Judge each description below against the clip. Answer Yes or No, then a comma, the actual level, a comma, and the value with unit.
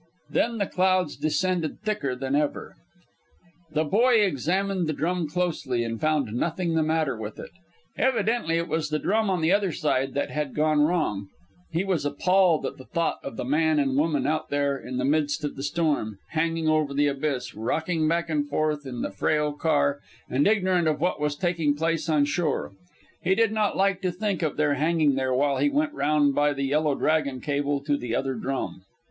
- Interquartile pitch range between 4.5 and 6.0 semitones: No, average, 3.6 semitones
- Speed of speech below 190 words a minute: No, average, 200 wpm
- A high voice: No, medium, 155 Hz